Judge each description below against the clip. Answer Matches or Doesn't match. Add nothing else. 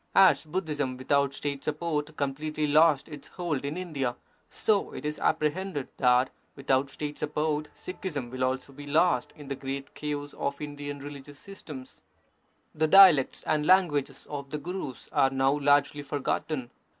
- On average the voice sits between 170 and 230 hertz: Doesn't match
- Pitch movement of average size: Doesn't match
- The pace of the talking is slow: Doesn't match